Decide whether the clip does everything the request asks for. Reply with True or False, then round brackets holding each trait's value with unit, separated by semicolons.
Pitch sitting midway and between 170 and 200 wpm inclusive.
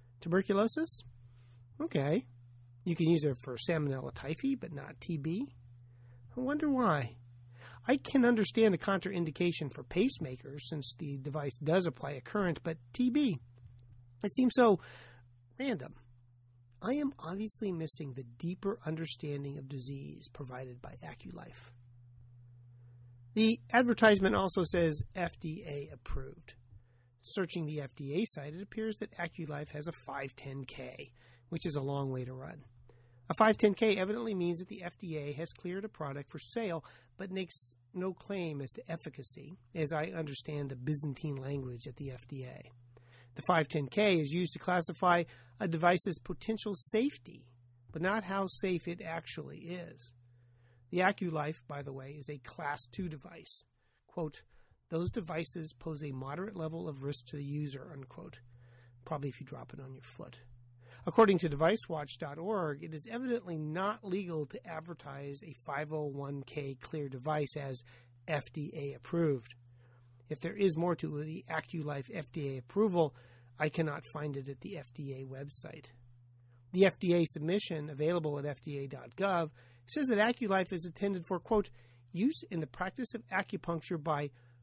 False (150 Hz; 145 wpm)